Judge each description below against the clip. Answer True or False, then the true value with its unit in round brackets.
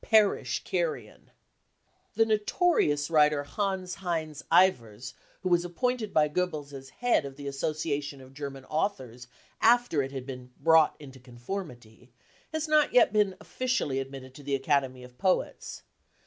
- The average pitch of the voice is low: False (150 Hz)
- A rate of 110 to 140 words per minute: False (155 wpm)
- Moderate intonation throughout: False (6.4 semitones)